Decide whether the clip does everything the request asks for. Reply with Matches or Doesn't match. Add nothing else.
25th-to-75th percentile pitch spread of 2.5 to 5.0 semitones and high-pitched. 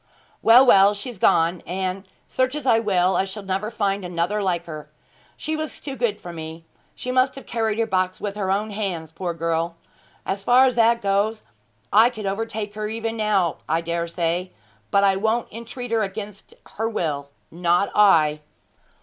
Matches